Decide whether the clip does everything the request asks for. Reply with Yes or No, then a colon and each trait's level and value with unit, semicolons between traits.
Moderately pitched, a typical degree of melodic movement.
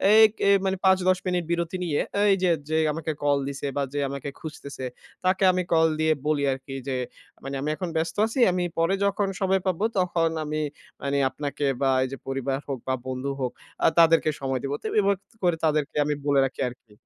Yes: medium, 155 Hz; average, 4.6 semitones